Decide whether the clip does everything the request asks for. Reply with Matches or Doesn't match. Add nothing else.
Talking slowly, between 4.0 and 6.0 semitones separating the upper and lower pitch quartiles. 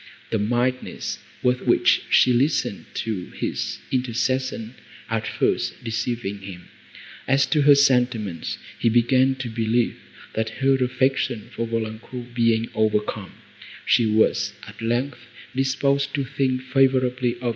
Doesn't match